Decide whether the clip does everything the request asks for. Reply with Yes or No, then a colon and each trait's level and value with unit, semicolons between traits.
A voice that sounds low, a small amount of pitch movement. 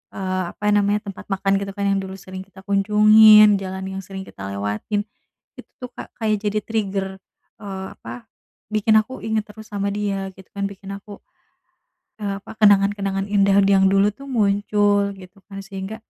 No: high, 200 Hz; narrow, 1.3 semitones